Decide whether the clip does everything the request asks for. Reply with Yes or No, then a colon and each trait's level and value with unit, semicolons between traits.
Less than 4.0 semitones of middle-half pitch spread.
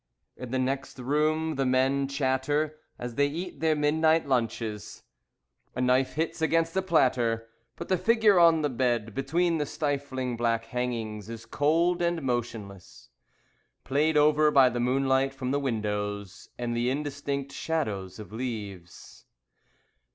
No: average, 4.4 semitones